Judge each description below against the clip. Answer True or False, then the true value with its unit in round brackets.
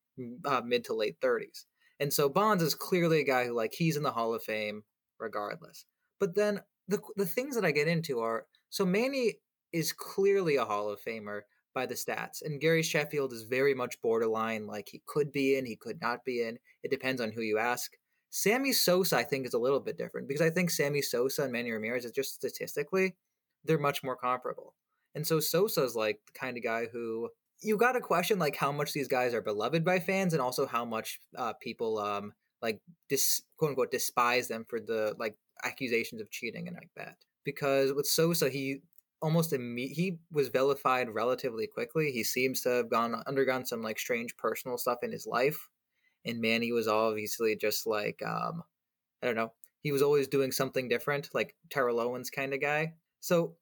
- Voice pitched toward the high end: False (140 Hz)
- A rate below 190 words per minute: False (205 wpm)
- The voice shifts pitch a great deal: True (6.7 semitones)